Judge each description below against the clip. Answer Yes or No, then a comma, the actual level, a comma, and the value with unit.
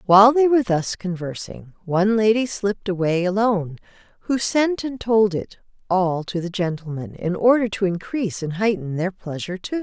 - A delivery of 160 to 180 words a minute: Yes, average, 170 wpm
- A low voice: No, high, 200 Hz